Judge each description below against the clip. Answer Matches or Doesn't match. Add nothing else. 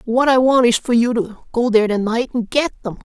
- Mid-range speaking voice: Doesn't match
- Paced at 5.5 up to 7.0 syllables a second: Matches